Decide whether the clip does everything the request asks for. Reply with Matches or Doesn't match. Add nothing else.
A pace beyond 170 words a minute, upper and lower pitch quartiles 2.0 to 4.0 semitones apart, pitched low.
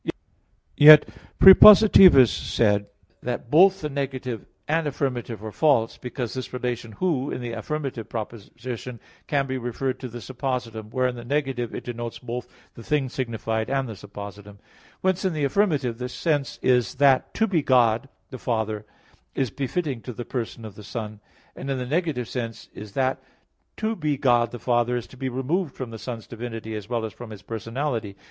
Matches